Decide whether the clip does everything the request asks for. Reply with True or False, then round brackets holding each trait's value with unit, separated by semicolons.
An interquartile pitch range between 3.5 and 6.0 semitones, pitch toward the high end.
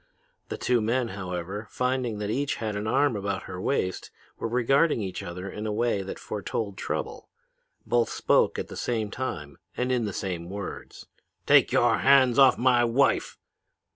False (4.2 semitones; 110 Hz)